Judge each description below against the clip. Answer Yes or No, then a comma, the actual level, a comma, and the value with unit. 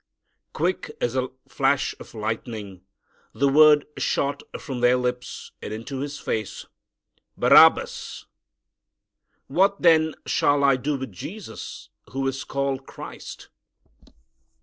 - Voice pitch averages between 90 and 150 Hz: Yes, low, 135 Hz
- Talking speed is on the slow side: Yes, slow, 115 wpm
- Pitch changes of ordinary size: Yes, average, 3.1 semitones